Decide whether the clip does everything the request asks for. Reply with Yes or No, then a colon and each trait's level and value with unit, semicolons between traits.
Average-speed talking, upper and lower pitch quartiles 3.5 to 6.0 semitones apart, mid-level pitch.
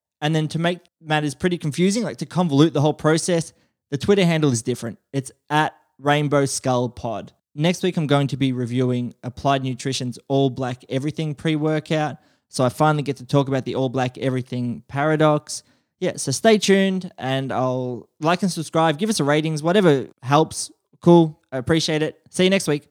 Yes: average, 190 wpm; average, 3.8 semitones; medium, 150 Hz